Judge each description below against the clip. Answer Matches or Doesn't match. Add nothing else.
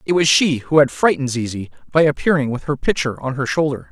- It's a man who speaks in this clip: Matches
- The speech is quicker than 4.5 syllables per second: Matches